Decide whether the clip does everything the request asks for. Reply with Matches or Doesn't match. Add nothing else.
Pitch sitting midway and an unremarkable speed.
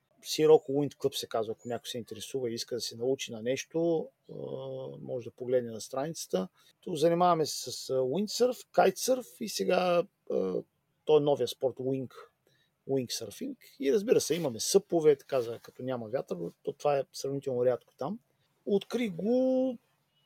Matches